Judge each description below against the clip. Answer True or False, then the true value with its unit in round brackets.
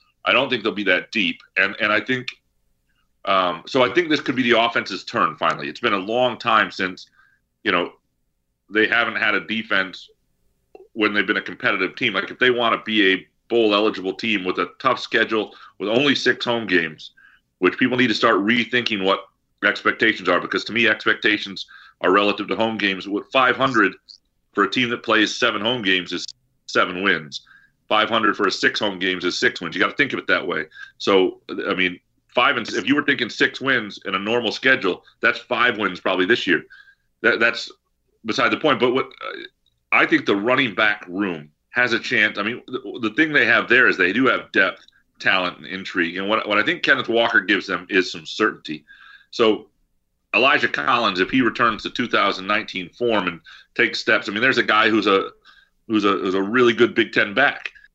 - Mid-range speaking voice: False (115 Hz)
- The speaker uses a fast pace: True (210 wpm)